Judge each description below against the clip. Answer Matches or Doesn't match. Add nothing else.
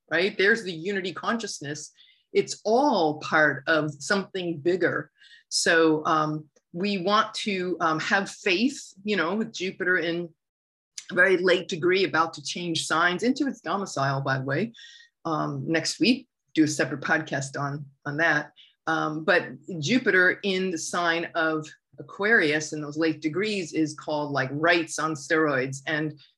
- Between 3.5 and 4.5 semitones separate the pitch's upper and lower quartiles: Matches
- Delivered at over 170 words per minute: Doesn't match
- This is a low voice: Doesn't match